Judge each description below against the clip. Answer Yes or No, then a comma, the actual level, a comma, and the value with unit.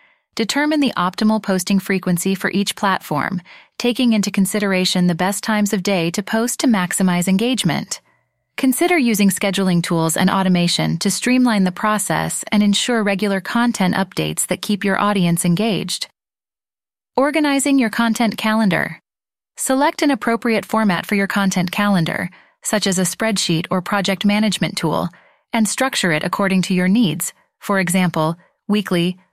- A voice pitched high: Yes, high, 200 Hz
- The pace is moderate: Yes, average, 145 wpm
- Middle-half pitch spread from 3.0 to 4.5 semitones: Yes, average, 3.4 semitones